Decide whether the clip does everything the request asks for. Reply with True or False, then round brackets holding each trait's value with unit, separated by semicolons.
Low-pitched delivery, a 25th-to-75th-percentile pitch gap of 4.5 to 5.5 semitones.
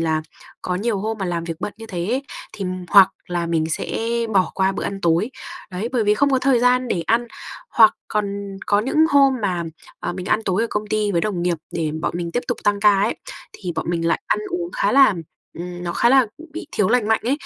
False (205 Hz; 5.0 semitones)